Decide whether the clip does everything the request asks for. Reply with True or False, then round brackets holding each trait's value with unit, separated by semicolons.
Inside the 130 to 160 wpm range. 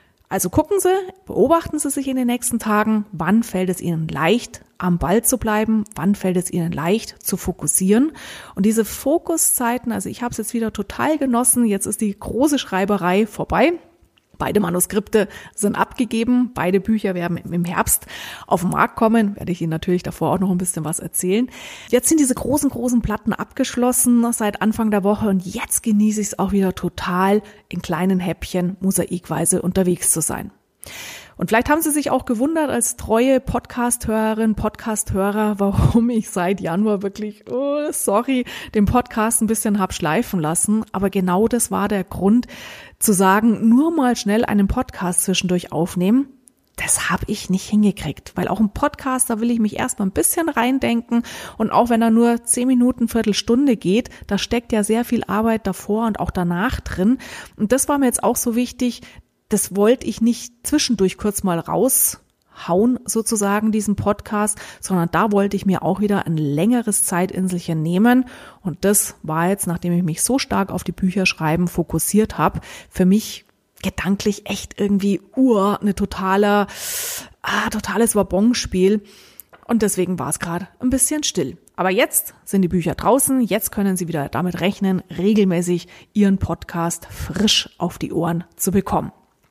False (170 wpm)